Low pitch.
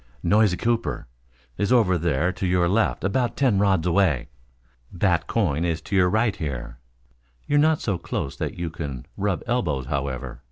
Yes: very low, 90 Hz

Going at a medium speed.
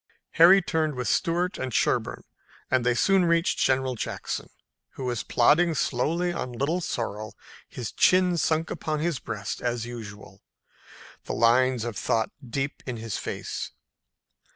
Yes: average, 145 wpm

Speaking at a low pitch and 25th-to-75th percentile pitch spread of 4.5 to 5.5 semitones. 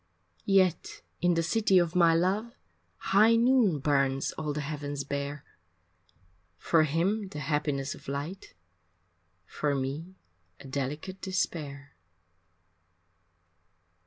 No: medium, 155 Hz; average, 4.9 semitones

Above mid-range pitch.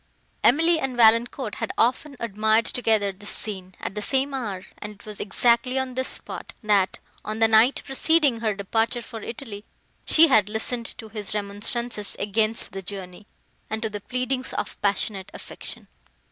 Yes: high, 220 Hz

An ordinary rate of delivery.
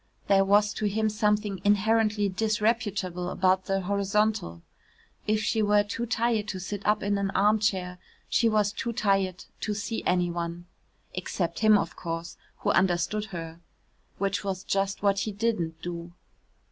Yes: average, 155 wpm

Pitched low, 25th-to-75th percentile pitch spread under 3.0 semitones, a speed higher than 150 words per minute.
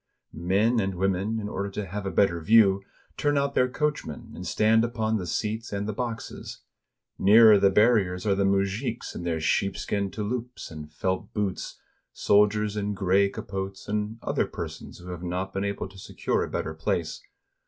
Yes: low, 100 Hz; narrow, 2.6 semitones; average, 180 wpm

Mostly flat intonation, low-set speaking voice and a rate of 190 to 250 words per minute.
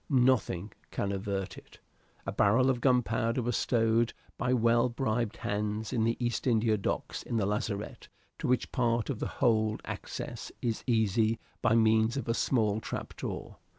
No: narrow, 2.1 semitones; low, 115 Hz; average, 165 wpm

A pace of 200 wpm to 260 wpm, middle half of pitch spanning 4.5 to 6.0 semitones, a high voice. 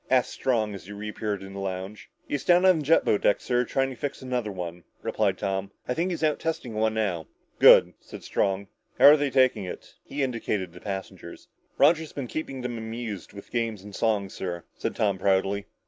No: fast, 205 wpm; average, 5.1 semitones; low, 110 Hz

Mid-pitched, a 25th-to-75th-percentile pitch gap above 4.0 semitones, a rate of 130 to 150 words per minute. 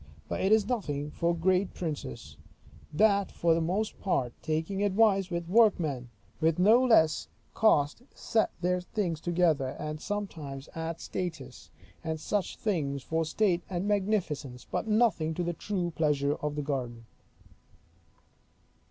Yes: medium, 170 Hz; average, 4.9 semitones; average, 140 wpm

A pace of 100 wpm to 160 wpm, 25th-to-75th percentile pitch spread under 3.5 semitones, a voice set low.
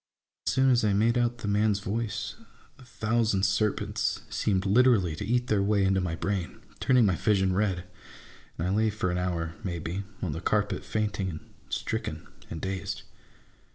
No: average, 180 wpm; average, 2.9 semitones; low, 100 Hz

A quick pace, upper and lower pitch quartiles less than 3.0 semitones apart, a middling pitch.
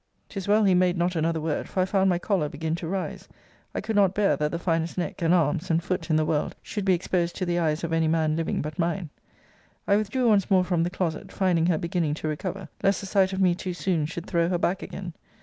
Yes: fast, 255 wpm; narrow, 2.6 semitones; medium, 175 Hz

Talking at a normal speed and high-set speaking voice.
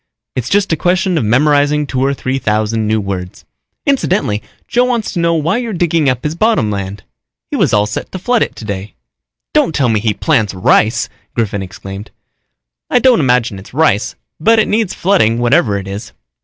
No: average, 190 wpm; low, 130 Hz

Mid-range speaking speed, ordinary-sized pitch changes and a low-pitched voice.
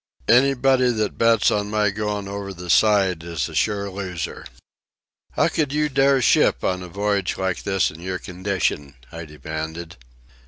Yes: average, 160 wpm; average, 3.6 semitones; low, 100 Hz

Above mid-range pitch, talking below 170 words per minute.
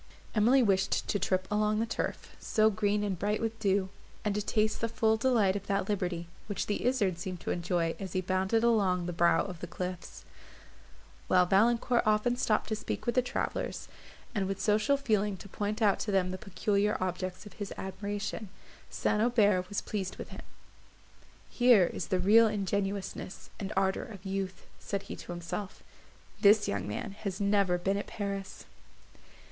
No: high, 200 Hz; average, 180 wpm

